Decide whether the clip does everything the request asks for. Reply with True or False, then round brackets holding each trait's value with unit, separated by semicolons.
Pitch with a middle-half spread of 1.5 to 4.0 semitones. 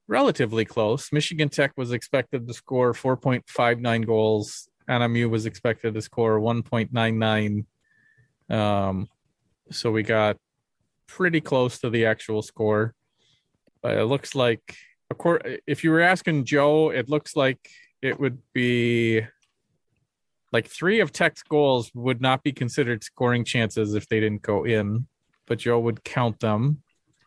True (3.7 semitones)